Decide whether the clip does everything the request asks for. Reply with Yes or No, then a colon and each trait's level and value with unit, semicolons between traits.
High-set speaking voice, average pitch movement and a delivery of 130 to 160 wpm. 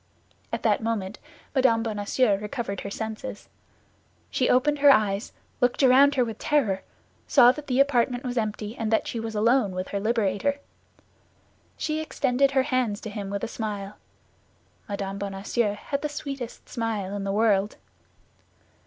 Yes: high, 225 Hz; average, 4.1 semitones; average, 155 wpm